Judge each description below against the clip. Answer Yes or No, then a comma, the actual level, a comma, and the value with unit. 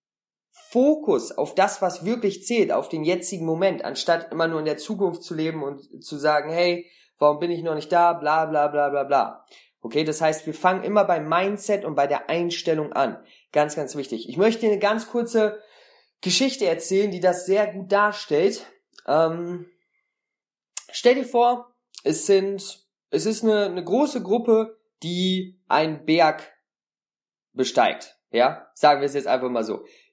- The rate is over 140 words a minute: Yes, average, 170 wpm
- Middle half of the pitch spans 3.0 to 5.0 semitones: No, wide, 5.4 semitones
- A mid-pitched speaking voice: Yes, medium, 180 Hz